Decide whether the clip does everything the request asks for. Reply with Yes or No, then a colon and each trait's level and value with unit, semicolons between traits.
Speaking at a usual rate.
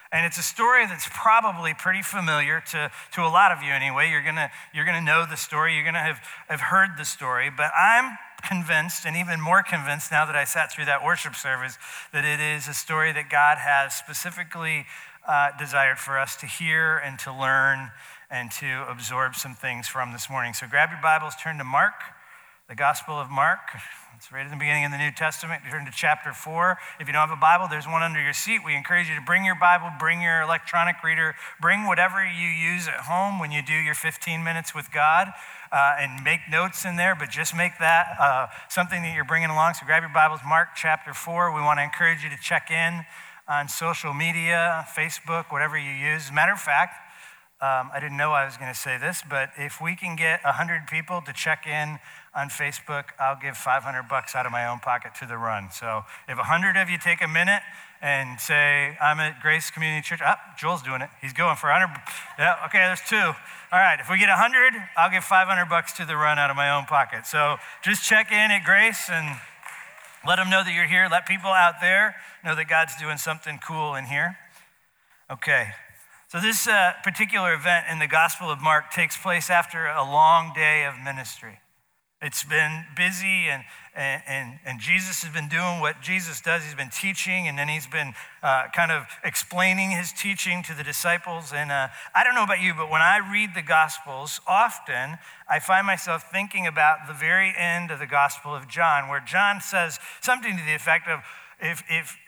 No: fast, 215 wpm